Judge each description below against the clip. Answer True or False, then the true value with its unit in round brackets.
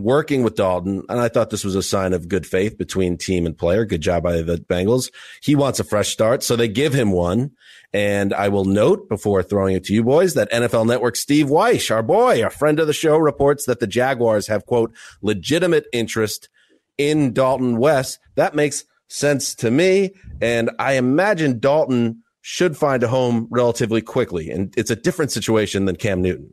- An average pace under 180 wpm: False (200 wpm)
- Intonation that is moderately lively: False (5.7 semitones)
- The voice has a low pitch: True (115 Hz)